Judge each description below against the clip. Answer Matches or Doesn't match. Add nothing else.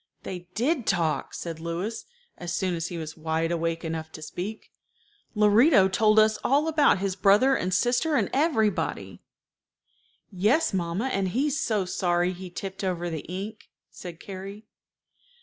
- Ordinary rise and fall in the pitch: Matches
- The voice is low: Doesn't match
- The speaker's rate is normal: Matches